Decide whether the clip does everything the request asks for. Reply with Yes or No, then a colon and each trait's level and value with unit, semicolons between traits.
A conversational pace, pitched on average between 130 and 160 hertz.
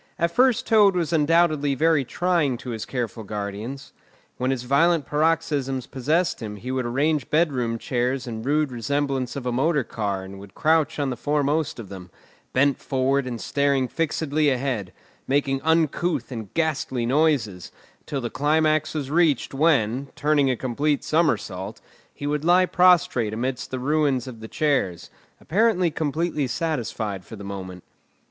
Yes: average, 155 wpm; medium, 140 Hz